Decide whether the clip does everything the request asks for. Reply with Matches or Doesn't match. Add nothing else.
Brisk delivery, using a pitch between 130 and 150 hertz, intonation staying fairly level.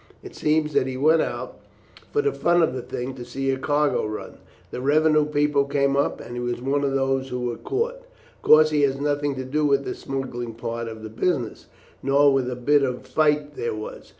Doesn't match